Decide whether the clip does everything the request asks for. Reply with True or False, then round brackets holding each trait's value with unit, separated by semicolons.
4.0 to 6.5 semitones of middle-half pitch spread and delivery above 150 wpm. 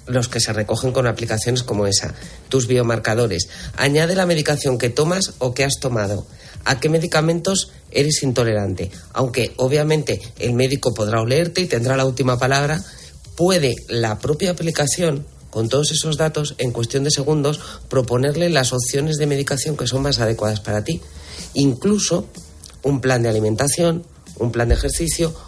True (4.6 semitones; 160 wpm)